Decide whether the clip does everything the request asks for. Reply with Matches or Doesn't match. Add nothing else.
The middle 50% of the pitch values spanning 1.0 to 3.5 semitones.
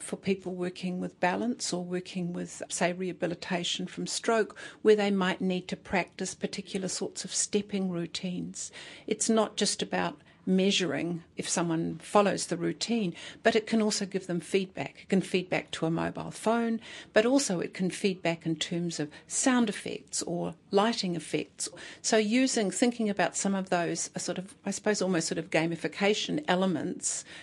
Matches